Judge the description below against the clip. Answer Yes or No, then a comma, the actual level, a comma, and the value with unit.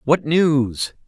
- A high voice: No, medium, 145 Hz